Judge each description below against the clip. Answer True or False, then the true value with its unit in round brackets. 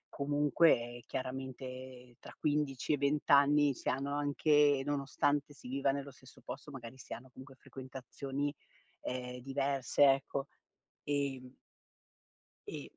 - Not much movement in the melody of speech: True (1.8 semitones)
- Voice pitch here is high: False (135 Hz)